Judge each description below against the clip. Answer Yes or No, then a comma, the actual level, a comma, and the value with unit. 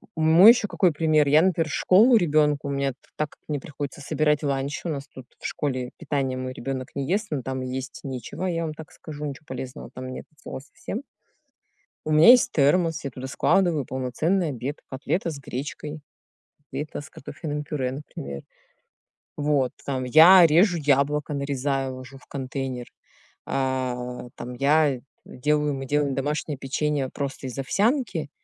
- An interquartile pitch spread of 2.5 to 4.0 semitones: Yes, average, 2.8 semitones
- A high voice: No, medium, 145 Hz